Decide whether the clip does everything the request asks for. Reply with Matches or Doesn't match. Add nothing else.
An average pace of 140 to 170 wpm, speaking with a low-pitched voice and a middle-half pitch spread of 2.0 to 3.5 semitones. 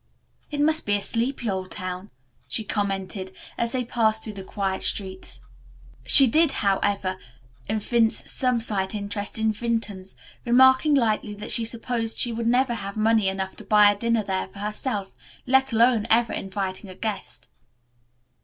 Doesn't match